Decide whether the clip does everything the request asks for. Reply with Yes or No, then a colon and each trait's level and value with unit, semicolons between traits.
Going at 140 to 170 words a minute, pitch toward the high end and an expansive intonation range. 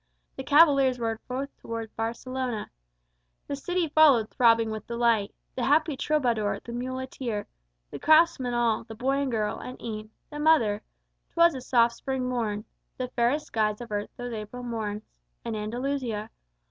No: average, 155 wpm; high, 240 Hz; average, 3.4 semitones